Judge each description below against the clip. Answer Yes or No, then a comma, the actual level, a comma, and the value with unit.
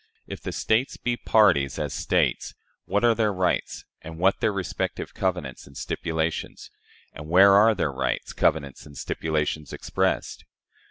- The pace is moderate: Yes, average, 150 wpm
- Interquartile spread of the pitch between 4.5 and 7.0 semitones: Yes, average, 5.2 semitones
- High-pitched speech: No, very low, 90 Hz